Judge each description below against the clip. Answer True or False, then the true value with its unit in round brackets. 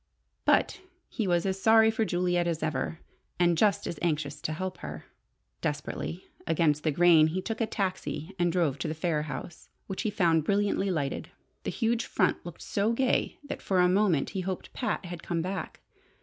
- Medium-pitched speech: True (175 Hz)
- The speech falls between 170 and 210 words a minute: True (190 wpm)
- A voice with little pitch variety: False (3.8 semitones)